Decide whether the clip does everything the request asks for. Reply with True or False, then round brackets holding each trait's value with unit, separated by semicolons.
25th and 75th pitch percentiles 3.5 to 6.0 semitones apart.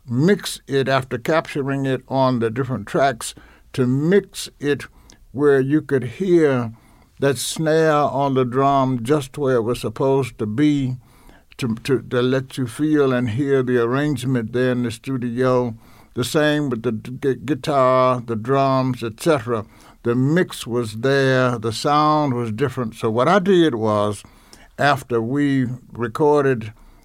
False (2.9 semitones)